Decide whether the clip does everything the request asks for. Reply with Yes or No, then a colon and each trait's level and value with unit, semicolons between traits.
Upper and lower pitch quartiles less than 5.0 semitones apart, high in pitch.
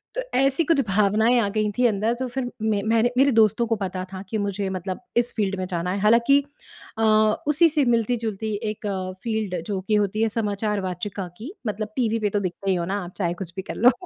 Yes: average, 3.3 semitones; high, 215 Hz